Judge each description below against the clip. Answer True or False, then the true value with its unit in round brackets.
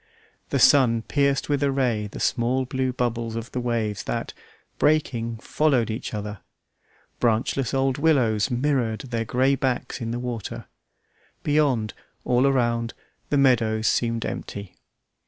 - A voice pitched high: False (120 Hz)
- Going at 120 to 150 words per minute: True (140 wpm)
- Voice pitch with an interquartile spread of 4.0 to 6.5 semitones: False (2.9 semitones)